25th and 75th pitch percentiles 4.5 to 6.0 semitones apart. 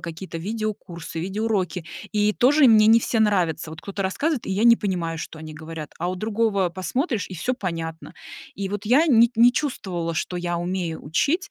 Yes: average, 5.0 semitones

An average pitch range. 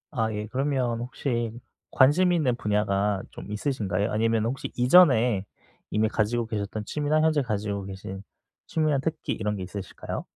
Yes: average, 4.5 semitones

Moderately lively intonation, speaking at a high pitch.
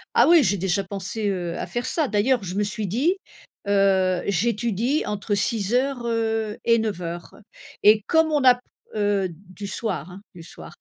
Yes: average, 3.6 semitones; high, 210 Hz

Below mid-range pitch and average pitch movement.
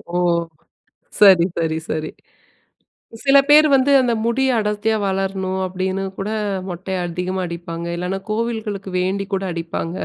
No: high, 190 Hz; average, 3.0 semitones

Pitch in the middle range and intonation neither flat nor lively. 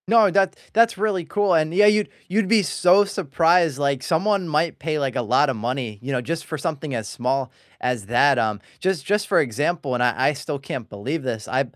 No: medium, 150 Hz; wide, 6.4 semitones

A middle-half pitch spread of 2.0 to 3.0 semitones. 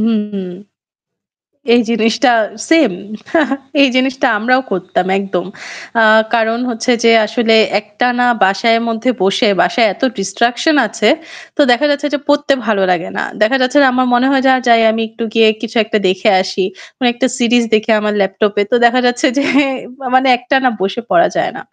No: average, 3.4 semitones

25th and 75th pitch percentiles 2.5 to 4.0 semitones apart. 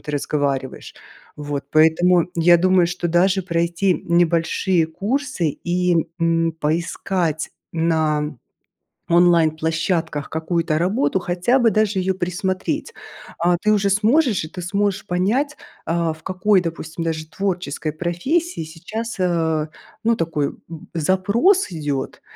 Yes: average, 3.0 semitones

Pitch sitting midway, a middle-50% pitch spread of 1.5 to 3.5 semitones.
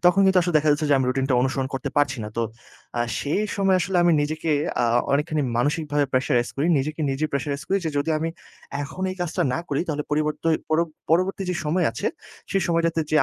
Yes: medium, 155 Hz; average, 3.1 semitones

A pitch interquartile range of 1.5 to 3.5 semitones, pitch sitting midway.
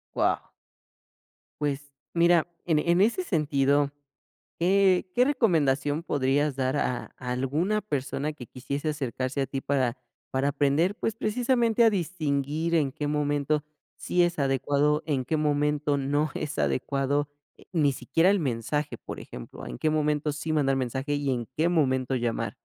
Yes: average, 3.2 semitones; medium, 145 Hz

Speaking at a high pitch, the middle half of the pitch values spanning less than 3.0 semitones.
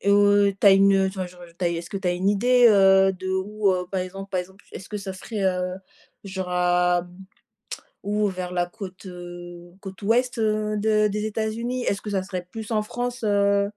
Yes: high, 195 Hz; narrow, 2.6 semitones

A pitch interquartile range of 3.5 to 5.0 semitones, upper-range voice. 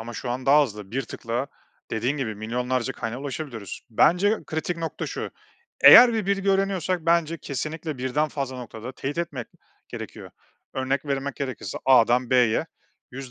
No: average, 4.5 semitones; low, 135 Hz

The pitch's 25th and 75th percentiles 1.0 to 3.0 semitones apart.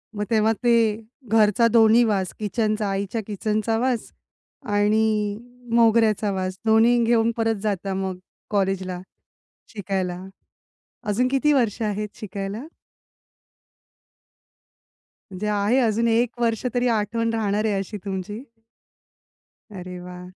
Yes: narrow, 2.5 semitones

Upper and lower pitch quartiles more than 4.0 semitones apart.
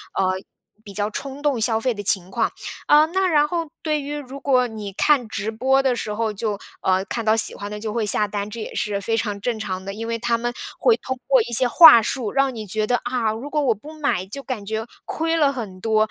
Yes: average, 4.5 semitones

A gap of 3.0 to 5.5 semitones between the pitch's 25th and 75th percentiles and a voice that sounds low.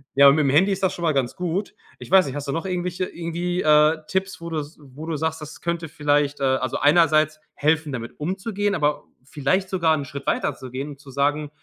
No: average, 3.6 semitones; medium, 155 Hz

